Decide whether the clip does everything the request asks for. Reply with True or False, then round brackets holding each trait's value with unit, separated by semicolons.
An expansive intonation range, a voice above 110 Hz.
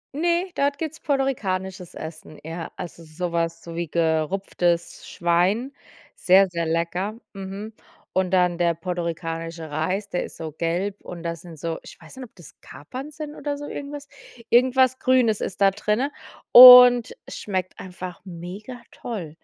True (6.6 semitones; 185 Hz)